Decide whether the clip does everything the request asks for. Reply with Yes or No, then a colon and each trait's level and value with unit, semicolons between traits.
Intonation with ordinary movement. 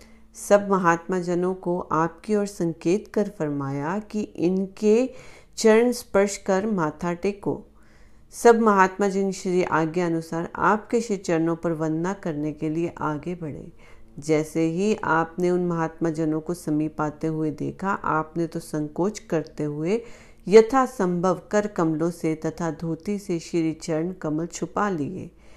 Yes: average, 3.8 semitones